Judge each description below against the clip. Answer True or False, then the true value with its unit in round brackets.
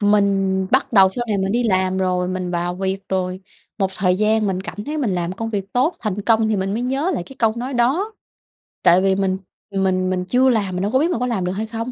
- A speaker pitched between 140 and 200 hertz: True (195 Hz)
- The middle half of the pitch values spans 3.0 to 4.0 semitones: True (3.7 semitones)